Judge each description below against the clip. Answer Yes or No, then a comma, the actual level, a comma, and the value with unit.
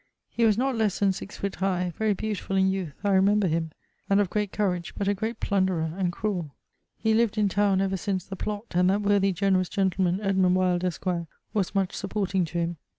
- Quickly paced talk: Yes, fast, 215 wpm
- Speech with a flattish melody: Yes, narrow, 2.1 semitones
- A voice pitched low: No, high, 195 Hz